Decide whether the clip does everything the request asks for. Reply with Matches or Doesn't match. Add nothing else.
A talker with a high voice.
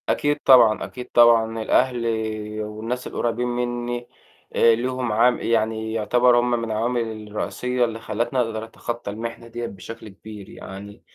Doesn't match